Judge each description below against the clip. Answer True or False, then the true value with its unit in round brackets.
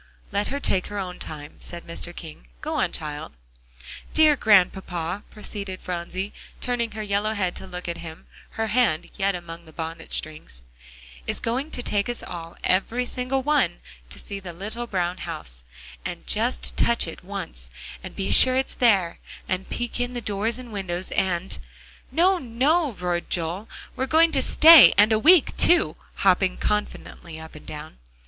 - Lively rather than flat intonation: True (6.0 semitones)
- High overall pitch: True (195 Hz)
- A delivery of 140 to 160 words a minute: False (170 wpm)